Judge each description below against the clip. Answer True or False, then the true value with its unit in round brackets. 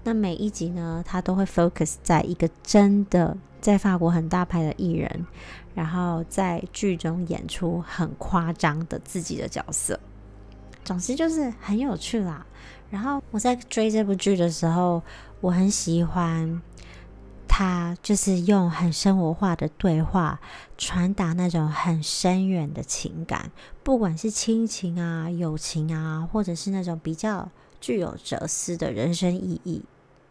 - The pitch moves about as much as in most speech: True (3.0 semitones)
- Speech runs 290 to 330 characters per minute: False (220 characters per minute)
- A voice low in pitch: False (175 Hz)